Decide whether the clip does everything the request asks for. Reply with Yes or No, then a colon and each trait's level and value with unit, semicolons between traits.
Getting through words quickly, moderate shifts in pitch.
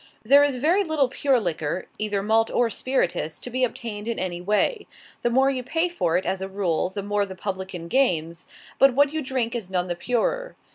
No: fast, 210 wpm; wide, 6.0 semitones